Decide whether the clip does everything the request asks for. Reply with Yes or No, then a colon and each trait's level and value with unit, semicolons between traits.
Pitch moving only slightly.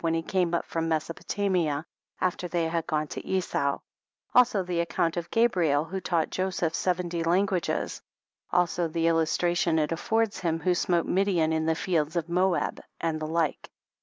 Yes: narrow, 2.0 semitones